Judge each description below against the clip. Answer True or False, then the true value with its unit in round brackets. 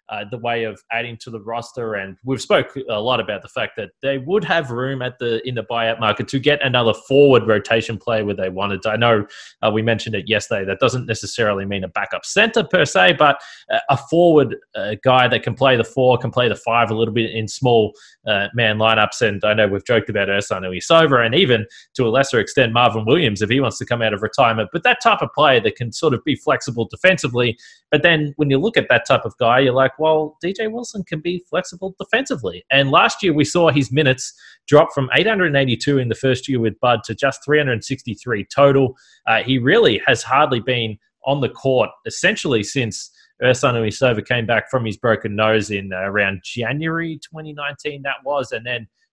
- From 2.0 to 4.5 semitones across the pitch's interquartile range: True (4.0 semitones)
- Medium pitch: False (125 Hz)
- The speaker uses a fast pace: True (220 wpm)